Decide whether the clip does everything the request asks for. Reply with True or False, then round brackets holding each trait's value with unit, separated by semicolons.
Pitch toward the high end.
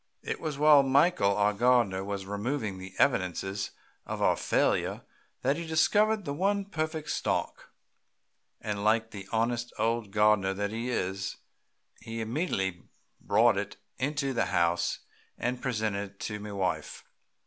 False (110 Hz)